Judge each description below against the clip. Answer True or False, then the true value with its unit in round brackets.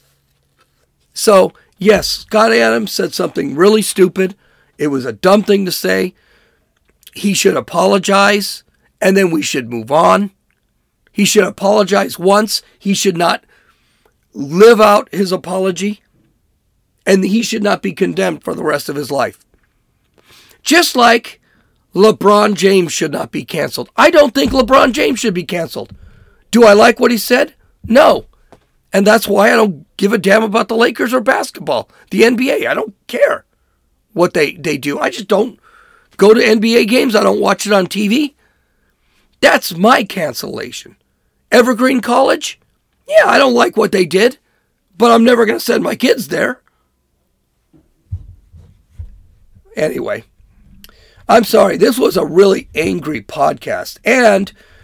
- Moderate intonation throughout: False (6.1 semitones)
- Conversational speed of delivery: True (150 wpm)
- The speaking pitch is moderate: False (200 Hz)